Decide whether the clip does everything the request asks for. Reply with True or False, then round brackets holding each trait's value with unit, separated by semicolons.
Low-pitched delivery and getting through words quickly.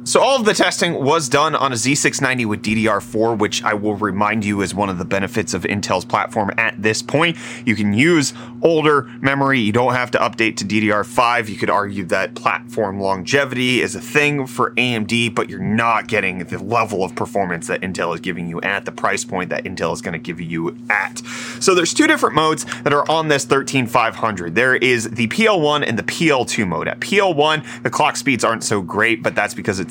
True (120 Hz; 215 wpm)